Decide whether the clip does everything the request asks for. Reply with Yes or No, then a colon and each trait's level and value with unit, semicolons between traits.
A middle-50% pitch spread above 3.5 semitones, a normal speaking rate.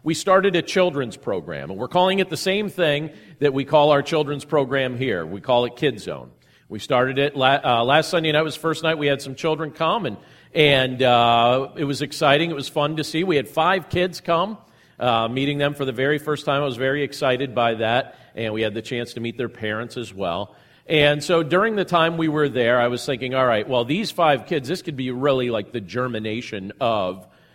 No: average, 4.4 semitones; fast, 230 wpm